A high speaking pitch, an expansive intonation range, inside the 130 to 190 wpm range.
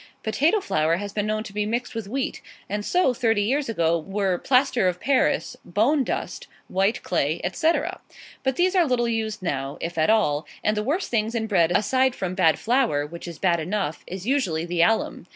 No: high, 210 Hz; wide, 6.2 semitones; average, 200 wpm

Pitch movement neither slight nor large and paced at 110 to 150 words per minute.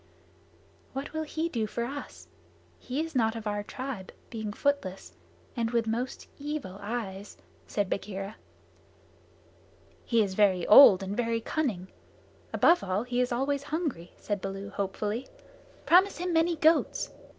No: wide, 5.8 semitones; average, 140 wpm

